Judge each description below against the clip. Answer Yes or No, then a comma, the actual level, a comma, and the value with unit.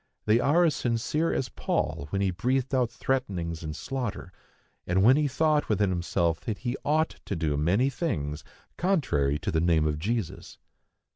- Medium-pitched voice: No, low, 105 Hz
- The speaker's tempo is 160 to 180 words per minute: Yes, average, 170 wpm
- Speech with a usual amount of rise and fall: No, wide, 8.1 semitones